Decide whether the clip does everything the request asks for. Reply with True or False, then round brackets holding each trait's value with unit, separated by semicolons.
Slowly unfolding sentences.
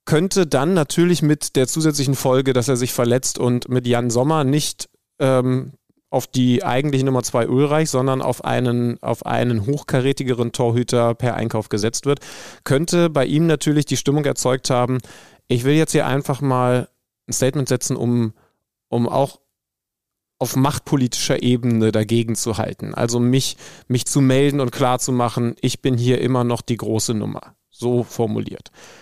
False (165 wpm)